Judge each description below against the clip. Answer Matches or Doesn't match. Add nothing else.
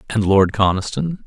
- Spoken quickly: Doesn't match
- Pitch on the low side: Matches